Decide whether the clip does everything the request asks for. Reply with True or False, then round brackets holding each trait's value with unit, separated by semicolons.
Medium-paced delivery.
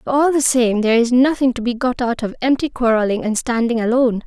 False (240 wpm)